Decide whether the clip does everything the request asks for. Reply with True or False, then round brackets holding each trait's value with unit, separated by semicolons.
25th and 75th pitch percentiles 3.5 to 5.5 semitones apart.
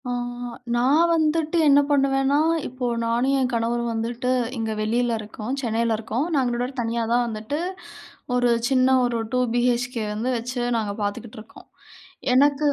False (2.8 semitones)